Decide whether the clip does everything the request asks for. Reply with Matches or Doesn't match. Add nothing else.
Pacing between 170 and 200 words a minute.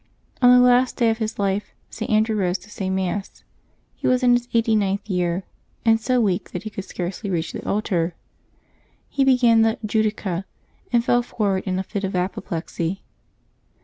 Matches